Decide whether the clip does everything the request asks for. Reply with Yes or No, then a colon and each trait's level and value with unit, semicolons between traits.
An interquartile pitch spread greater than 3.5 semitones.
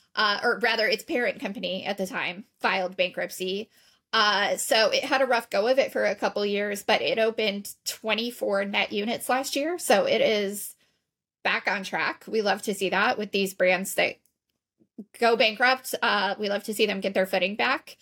No: average, 2.9 semitones